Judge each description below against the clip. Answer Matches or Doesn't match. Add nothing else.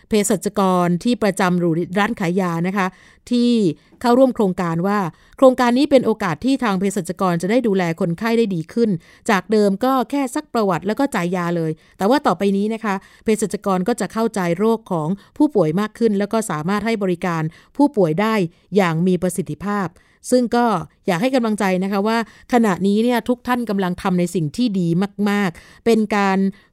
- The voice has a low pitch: Doesn't match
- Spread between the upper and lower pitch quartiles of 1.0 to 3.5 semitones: Doesn't match